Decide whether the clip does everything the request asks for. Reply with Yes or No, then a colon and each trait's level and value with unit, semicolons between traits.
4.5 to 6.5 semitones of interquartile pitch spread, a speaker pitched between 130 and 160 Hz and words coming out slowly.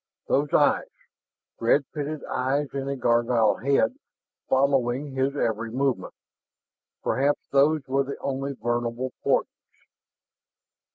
No: narrow, 2.6 semitones; low, 135 Hz; slow, 110 wpm